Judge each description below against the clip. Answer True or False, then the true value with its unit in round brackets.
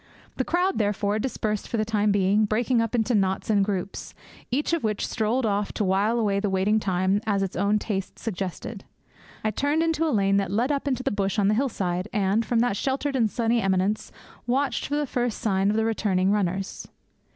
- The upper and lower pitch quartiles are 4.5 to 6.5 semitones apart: False (3.4 semitones)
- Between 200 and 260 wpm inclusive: True (205 wpm)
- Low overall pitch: False (210 Hz)